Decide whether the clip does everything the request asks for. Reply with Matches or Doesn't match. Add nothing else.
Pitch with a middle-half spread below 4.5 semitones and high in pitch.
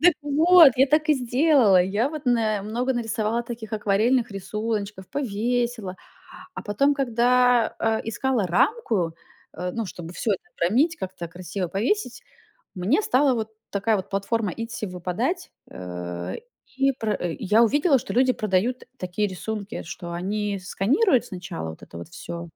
Doesn't match